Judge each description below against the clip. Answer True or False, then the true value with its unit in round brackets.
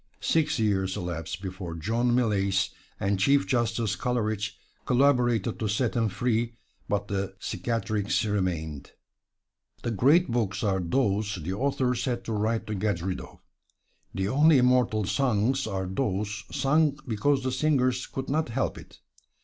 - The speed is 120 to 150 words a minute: True (145 wpm)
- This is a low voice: True (110 Hz)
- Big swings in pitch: False (4.4 semitones)